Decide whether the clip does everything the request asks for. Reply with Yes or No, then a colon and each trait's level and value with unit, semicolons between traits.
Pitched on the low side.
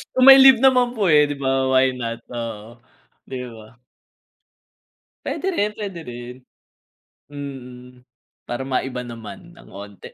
Yes: low, 130 Hz